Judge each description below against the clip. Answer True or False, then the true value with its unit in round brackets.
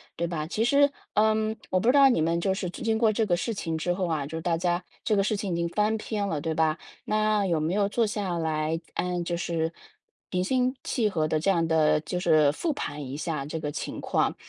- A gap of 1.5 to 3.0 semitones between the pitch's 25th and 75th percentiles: False (4.8 semitones)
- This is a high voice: False (175 Hz)